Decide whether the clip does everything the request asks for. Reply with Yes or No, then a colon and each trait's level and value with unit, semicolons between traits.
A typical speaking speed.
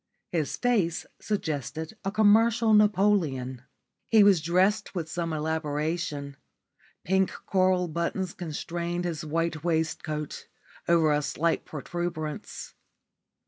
No: slow, 100 wpm